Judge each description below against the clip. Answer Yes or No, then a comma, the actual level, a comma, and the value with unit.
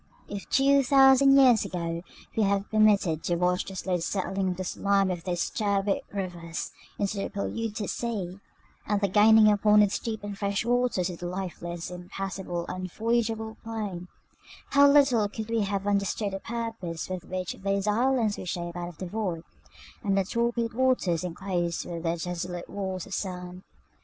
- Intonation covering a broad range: No, average, 3.6 semitones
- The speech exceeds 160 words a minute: Yes, average, 170 wpm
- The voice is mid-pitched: No, high, 195 Hz